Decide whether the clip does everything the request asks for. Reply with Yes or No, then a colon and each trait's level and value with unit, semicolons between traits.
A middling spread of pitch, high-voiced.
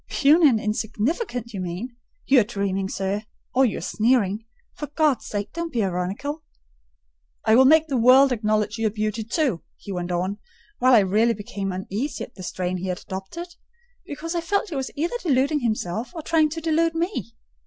No: wide, 6.8 semitones; high, 230 Hz